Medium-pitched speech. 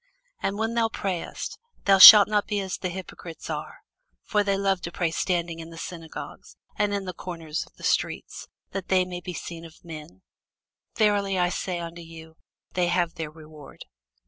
Yes: medium, 180 Hz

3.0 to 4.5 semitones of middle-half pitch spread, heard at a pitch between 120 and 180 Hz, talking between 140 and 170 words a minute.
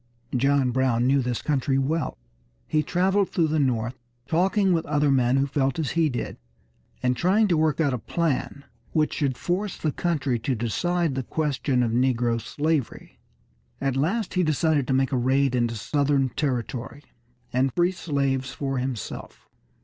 Yes: average, 3.8 semitones; medium, 140 Hz; average, 165 wpm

